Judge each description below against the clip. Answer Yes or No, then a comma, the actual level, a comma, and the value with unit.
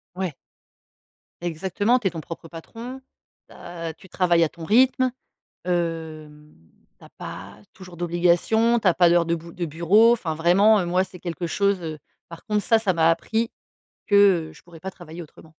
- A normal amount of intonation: Yes, average, 3.5 semitones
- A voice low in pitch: No, medium, 175 Hz